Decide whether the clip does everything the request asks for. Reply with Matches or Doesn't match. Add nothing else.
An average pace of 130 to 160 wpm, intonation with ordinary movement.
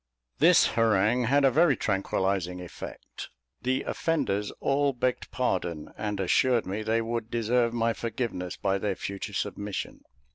Matches